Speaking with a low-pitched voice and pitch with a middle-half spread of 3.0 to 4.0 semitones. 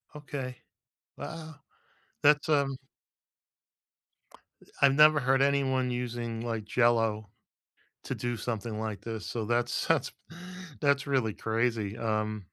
Yes: low, 120 Hz; average, 3.7 semitones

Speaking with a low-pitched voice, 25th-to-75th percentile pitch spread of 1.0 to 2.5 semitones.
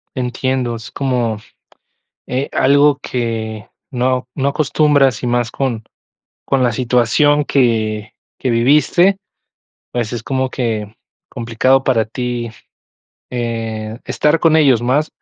No: low, 125 Hz; average, 2.9 semitones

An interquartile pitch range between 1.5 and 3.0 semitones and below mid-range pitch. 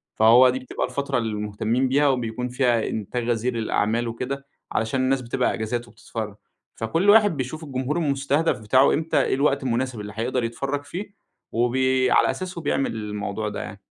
No: average, 3.4 semitones; low, 125 Hz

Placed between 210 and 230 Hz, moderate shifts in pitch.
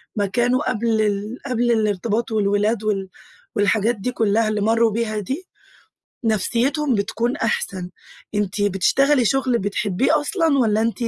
Yes: high, 225 Hz; average, 3.3 semitones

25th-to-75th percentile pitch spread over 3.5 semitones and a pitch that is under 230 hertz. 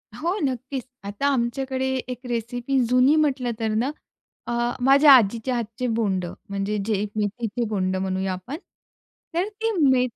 No: average, 4.0 semitones; high, 240 Hz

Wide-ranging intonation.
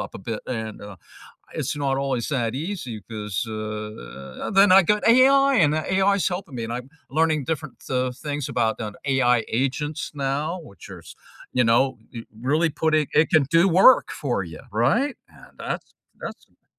Yes: wide, 6.1 semitones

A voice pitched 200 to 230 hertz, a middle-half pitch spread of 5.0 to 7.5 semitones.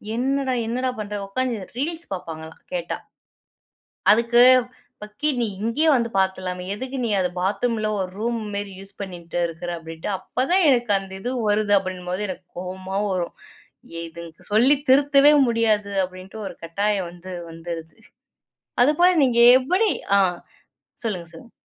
Yes: high, 205 Hz; average, 5.3 semitones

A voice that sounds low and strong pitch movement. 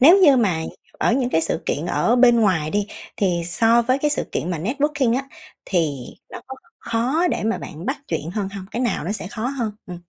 No: high, 225 Hz; wide, 6.3 semitones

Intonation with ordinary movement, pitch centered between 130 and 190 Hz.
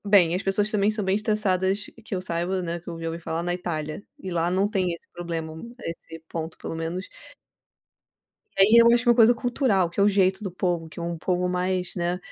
Yes: average, 3.0 semitones; medium, 185 Hz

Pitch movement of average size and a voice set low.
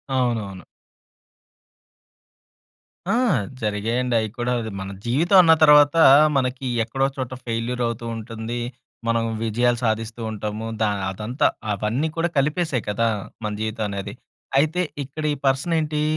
Yes: average, 4.0 semitones; low, 120 Hz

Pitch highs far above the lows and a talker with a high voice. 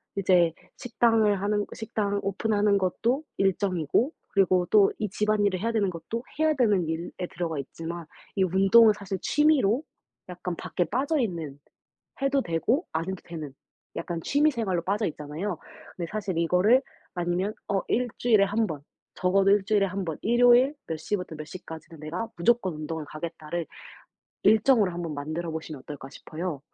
No: average, 4.5 semitones; high, 195 Hz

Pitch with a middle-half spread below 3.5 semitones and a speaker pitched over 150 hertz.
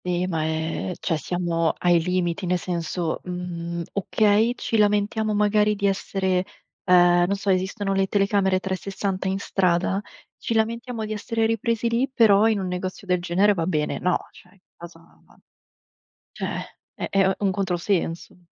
Yes: average, 2.7 semitones; high, 190 Hz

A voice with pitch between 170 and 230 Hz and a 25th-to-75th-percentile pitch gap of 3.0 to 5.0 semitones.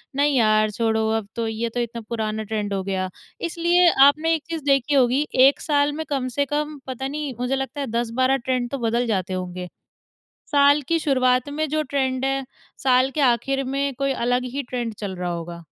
No: very high, 255 Hz; average, 4.2 semitones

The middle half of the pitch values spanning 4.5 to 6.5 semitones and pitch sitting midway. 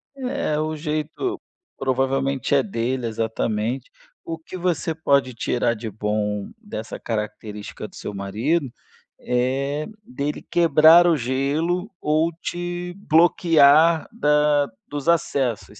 Yes: average, 5.3 semitones; medium, 145 Hz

